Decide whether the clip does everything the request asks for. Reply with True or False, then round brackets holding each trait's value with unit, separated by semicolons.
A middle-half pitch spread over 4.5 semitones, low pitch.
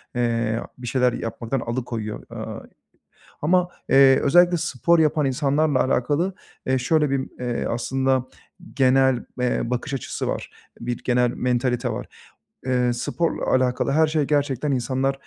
False (2.7 semitones; 130 Hz)